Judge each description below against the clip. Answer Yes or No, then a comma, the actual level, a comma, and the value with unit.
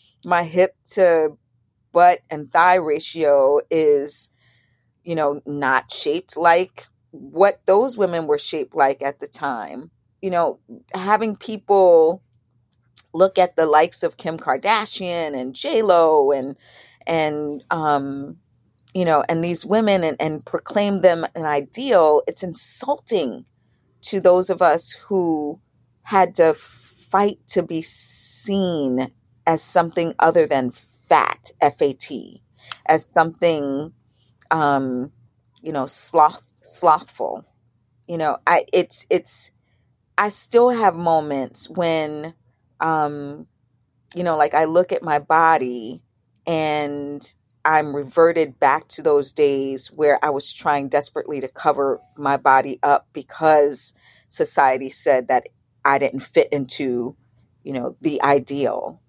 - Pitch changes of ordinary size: Yes, average, 4.8 semitones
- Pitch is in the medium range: Yes, medium, 150 Hz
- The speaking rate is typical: No, slow, 125 wpm